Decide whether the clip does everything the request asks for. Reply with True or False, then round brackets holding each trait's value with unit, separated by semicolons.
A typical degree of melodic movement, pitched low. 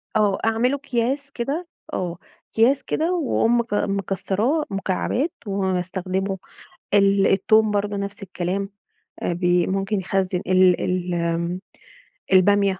False (3.4 semitones; 195 Hz)